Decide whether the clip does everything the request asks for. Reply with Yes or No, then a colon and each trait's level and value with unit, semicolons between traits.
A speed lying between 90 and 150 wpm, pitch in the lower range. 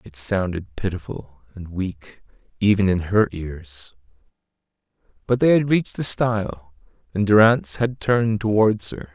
Yes: average, 140 wpm; low, 100 Hz